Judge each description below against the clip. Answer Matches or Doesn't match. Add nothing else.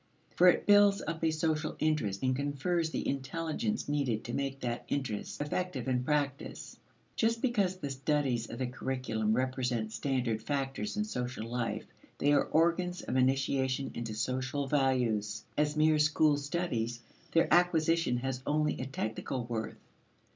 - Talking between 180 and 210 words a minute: Doesn't match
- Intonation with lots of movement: Doesn't match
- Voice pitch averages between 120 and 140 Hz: Matches